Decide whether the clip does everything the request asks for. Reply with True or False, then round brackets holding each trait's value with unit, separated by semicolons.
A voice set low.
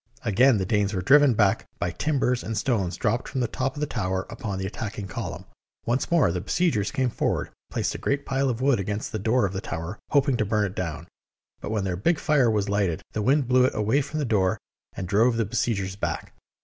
True (110 Hz)